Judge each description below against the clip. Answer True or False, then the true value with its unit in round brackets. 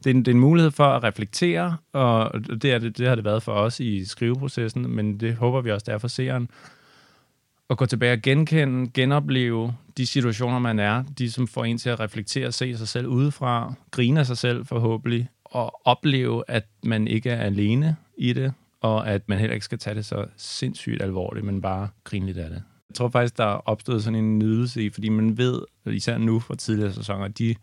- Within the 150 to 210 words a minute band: False (225 wpm)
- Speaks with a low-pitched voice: True (120 Hz)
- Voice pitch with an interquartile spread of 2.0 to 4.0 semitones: True (2.8 semitones)